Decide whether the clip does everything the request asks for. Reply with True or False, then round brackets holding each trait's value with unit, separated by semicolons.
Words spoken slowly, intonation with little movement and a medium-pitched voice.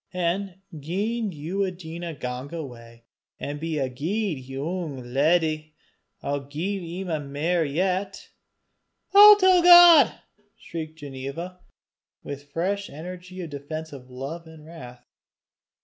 False (115 wpm; 4.6 semitones; 160 Hz)